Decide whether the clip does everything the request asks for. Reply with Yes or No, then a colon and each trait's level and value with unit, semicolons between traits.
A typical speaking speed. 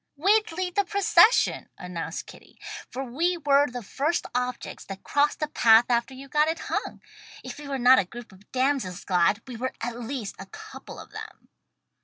Yes: average, 190 wpm